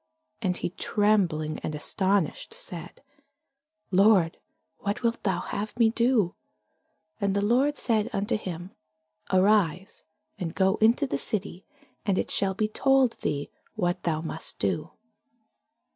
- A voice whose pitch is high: Yes, high, 200 Hz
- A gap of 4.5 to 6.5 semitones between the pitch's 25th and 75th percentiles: No, average, 3.9 semitones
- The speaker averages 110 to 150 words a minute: Yes, slow, 135 wpm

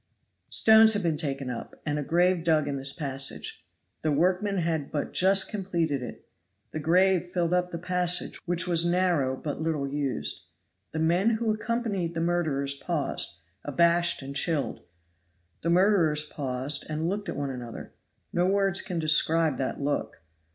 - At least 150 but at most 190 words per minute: Yes, average, 165 wpm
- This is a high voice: No, medium, 165 Hz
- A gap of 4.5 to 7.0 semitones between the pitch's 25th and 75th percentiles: No, average, 4.0 semitones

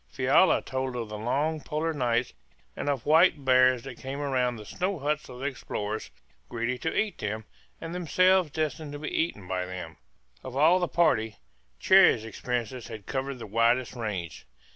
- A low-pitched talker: Yes, low, 130 Hz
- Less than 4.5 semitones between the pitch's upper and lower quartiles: No, average, 5.1 semitones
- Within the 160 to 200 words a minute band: Yes, average, 175 wpm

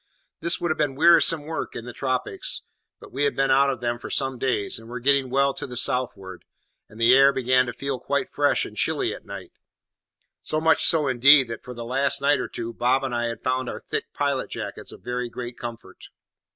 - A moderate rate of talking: No, fast, 225 wpm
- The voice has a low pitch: Yes, low, 130 Hz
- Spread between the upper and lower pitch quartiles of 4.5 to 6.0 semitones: No, narrow, 2.6 semitones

